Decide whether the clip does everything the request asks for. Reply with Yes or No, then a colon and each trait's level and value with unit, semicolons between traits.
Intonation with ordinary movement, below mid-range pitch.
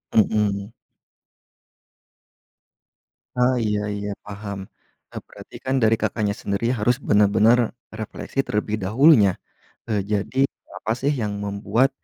Yes: average, 3.1 semitones; low, 105 Hz